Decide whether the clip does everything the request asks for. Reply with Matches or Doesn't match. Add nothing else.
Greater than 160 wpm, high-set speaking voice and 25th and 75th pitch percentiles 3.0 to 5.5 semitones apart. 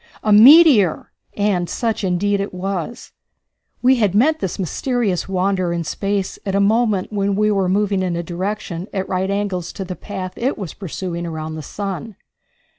Doesn't match